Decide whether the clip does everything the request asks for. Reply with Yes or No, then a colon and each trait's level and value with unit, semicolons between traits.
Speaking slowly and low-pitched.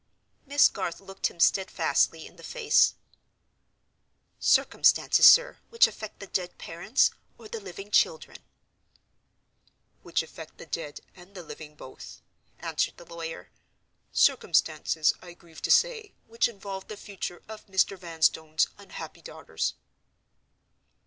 No: slow, 125 wpm; high, 190 Hz